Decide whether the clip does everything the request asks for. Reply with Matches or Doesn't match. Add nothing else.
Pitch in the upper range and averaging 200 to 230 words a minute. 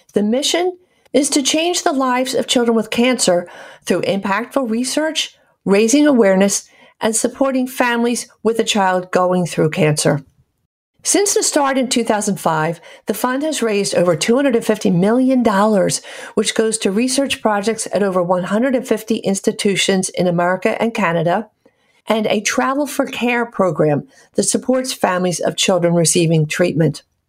Doesn't match